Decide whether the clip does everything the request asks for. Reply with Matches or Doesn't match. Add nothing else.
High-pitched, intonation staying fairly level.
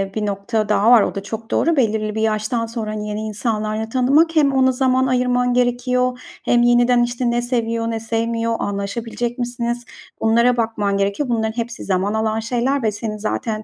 Matches